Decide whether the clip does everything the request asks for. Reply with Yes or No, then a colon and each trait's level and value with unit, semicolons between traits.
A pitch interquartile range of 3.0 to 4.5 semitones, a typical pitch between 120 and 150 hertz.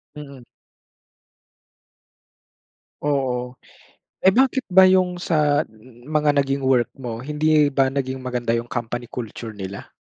Yes: average, 3.5 semitones; low, 135 Hz